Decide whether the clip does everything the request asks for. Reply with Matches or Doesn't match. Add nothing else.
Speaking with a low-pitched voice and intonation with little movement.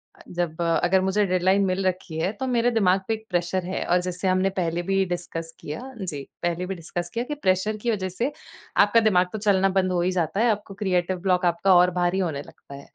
Doesn't match